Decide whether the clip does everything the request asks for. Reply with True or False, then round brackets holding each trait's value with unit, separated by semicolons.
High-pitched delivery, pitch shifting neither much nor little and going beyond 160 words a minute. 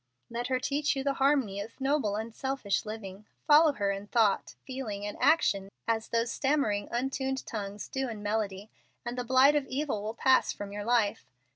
True (230 Hz; 4.6 semitones; 180 wpm)